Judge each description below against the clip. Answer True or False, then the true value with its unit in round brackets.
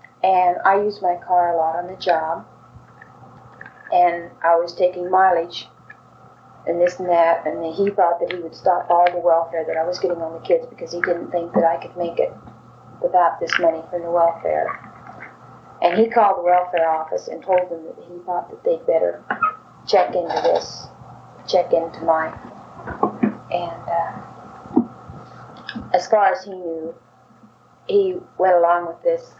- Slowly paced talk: False (170 wpm)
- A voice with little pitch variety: True (1.9 semitones)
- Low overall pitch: False (175 Hz)